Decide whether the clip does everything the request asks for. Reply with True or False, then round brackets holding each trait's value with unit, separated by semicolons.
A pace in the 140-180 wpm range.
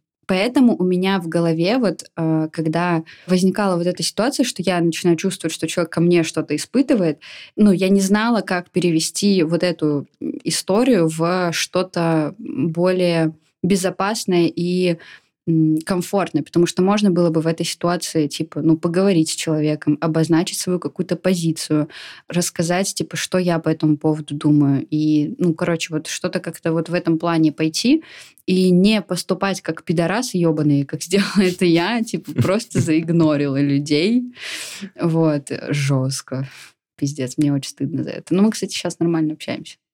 True (150 wpm)